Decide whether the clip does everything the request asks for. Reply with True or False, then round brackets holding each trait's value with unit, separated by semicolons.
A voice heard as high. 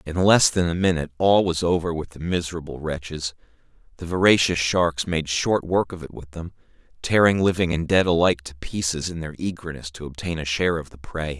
False (85 Hz)